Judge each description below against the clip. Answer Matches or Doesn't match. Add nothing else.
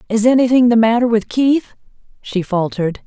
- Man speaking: Doesn't match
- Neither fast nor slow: Matches